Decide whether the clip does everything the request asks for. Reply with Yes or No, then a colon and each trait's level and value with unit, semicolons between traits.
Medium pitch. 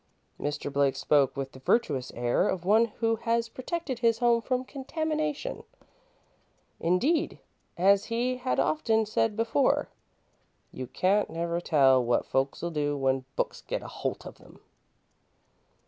No: high, 210 Hz